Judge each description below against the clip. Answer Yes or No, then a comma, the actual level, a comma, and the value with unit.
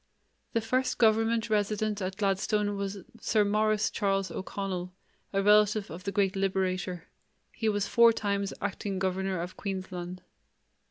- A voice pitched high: Yes, high, 200 Hz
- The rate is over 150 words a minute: No, average, 140 wpm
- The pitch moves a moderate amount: No, narrow, 2.0 semitones